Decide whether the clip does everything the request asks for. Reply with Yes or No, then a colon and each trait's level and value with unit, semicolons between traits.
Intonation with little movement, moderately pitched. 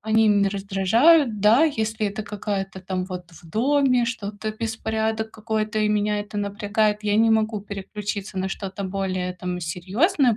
No: narrow, 2.3 semitones; high, 210 Hz